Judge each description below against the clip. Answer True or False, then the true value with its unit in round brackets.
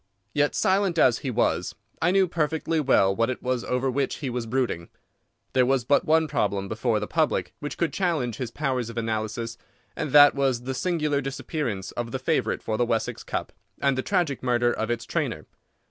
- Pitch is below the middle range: True (130 Hz)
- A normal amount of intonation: True (4.3 semitones)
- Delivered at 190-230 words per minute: True (195 wpm)